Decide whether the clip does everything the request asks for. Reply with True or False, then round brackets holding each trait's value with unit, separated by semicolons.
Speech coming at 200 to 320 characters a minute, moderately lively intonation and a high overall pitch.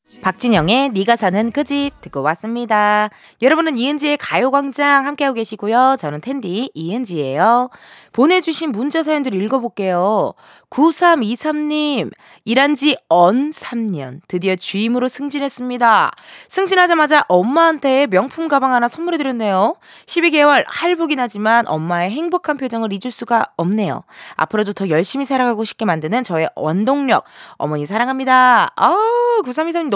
False (315 characters per minute; 5.8 semitones; 250 Hz)